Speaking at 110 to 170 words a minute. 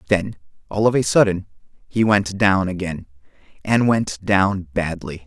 Yes: average, 150 wpm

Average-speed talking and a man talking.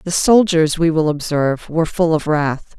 No: average, 195 wpm; female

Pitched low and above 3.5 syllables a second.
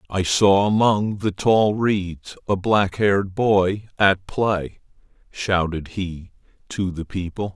No: low, 100 Hz; 3.4 syllables/s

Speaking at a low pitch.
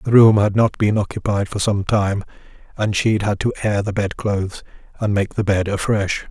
Yes: low, 100 Hz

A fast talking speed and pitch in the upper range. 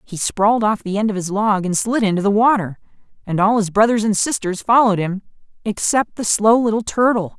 Yes: fast, 210 wpm; high, 210 Hz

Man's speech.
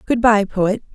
No: female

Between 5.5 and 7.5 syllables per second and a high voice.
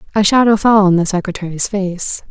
Yes: 5.6 syllables/s; high, 195 Hz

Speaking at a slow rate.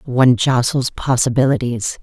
Yes: slow, 90 wpm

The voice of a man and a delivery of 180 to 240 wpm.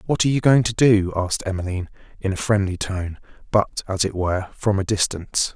Yes: male; fast, 205 wpm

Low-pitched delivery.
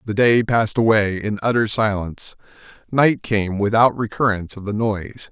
Yes: low, 105 Hz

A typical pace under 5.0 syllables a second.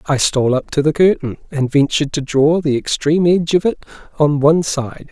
No: 5.8 syllables/s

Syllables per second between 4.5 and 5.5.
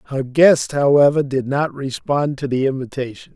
Yes: 4.8 syllables/s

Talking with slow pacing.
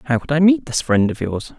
No: fast, 305 wpm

